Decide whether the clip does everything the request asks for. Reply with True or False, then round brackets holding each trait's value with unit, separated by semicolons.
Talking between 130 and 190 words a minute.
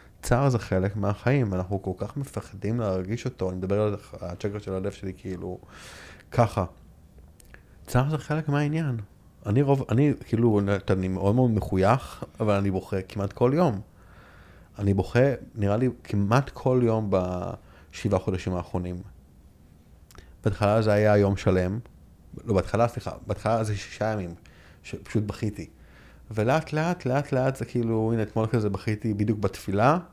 True (145 wpm)